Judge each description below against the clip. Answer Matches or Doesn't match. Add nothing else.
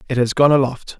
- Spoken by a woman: Doesn't match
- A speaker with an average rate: Doesn't match